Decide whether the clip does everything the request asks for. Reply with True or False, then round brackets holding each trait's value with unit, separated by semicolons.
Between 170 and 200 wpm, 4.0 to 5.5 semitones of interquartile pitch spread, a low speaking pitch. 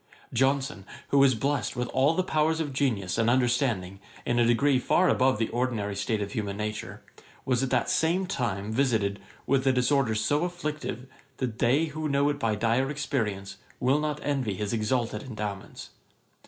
True (175 wpm; 4.5 semitones; 125 Hz)